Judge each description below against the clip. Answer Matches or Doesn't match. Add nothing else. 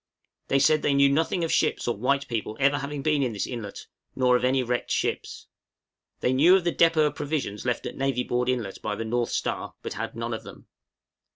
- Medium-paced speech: Doesn't match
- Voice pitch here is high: Doesn't match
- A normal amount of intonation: Matches